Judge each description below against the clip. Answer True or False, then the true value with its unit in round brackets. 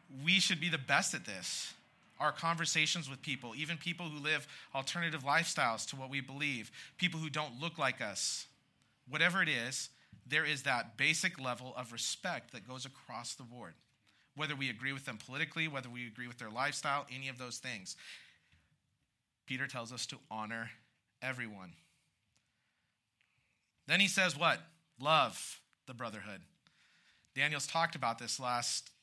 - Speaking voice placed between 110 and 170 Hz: True (135 Hz)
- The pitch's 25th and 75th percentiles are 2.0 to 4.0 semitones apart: False (4.4 semitones)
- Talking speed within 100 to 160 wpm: True (155 wpm)